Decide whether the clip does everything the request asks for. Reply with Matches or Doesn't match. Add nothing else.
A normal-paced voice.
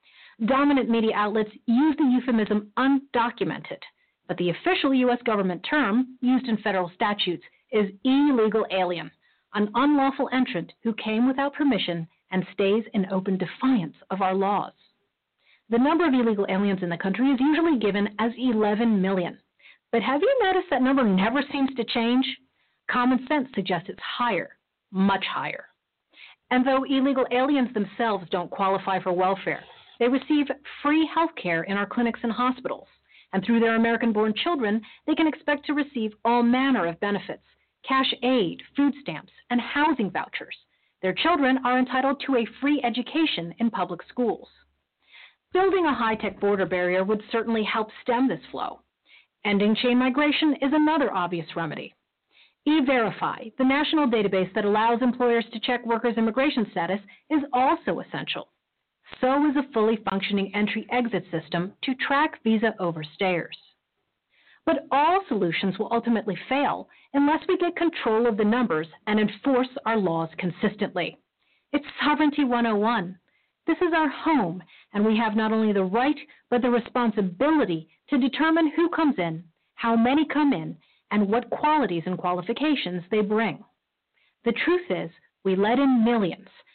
Matches